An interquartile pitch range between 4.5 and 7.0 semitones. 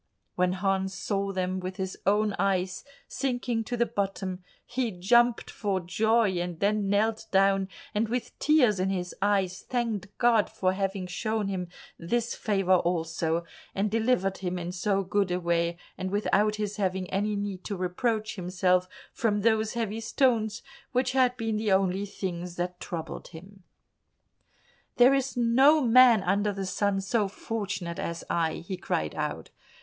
No: average, 3.2 semitones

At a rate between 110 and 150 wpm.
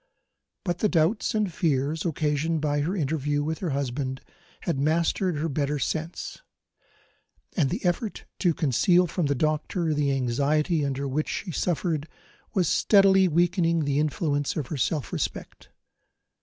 Yes: average, 145 wpm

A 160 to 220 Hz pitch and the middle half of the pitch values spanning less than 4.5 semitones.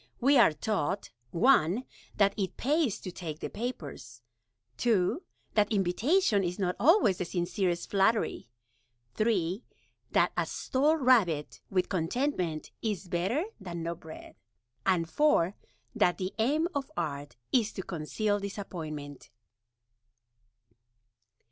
No: high, 190 Hz; wide, 5.4 semitones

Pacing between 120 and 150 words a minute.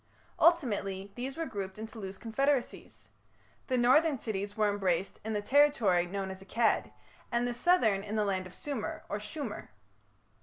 No: average, 160 wpm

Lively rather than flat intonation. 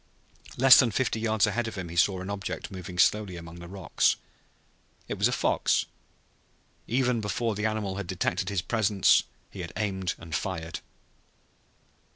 No: average, 3.3 semitones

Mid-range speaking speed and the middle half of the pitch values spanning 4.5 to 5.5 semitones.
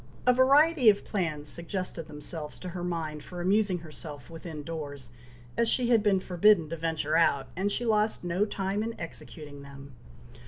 Yes: average, 170 wpm; average, 5.2 semitones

